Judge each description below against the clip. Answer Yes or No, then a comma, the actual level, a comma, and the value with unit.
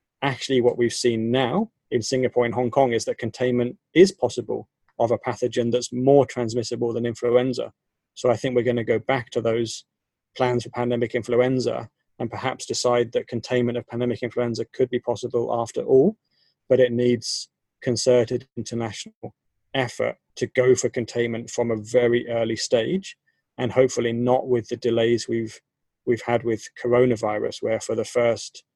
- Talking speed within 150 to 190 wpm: Yes, average, 165 wpm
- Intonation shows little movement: Yes, narrow, 1.1 semitones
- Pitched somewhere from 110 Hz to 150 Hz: Yes, low, 120 Hz